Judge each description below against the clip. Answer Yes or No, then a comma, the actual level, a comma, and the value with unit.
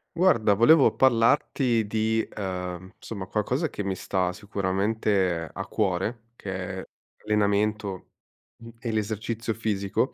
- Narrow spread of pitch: No, average, 3.0 semitones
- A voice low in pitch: Yes, low, 105 Hz